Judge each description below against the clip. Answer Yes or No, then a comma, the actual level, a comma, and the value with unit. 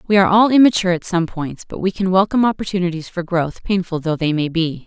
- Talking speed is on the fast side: Yes, fast, 235 wpm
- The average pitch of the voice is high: No, medium, 180 Hz